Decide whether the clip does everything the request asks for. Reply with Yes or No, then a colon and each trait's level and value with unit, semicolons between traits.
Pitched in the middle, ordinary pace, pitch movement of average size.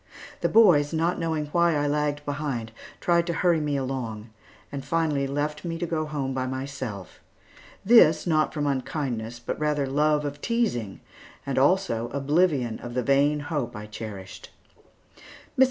Yes: medium, 145 Hz; average, 155 wpm; average, 3.3 semitones